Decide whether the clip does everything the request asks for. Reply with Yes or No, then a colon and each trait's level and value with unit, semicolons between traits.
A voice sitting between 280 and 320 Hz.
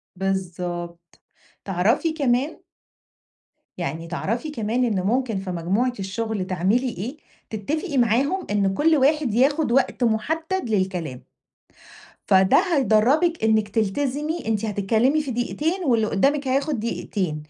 No: high, 225 Hz